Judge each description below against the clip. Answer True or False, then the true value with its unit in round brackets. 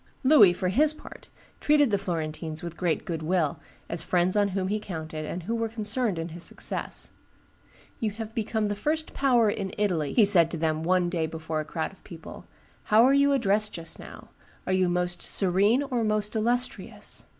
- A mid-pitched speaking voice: False (195 Hz)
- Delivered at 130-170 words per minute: False (195 wpm)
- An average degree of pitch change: True (4.9 semitones)